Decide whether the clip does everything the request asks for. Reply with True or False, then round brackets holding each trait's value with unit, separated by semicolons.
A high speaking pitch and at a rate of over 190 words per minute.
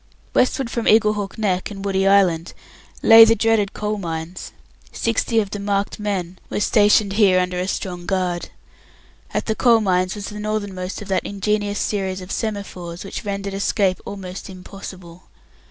False (200 Hz; 160 wpm)